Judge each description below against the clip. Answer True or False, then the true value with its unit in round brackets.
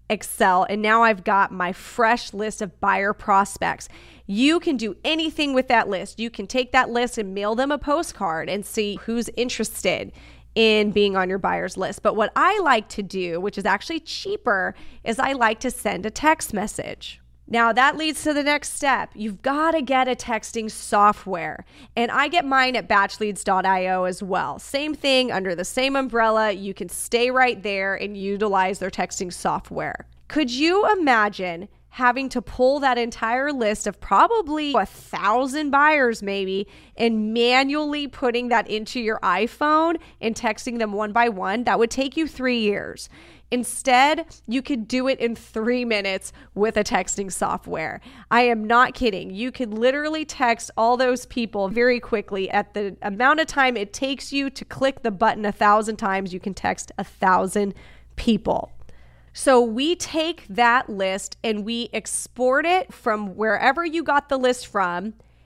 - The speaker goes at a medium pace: True (175 wpm)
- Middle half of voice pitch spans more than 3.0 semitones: True (4.3 semitones)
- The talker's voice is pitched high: True (230 Hz)